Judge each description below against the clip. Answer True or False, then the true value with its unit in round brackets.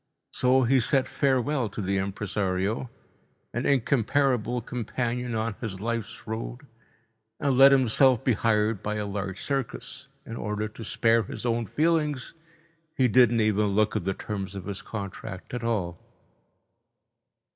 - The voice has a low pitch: True (115 Hz)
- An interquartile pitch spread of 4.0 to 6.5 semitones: False (3.6 semitones)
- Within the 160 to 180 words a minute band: False (145 wpm)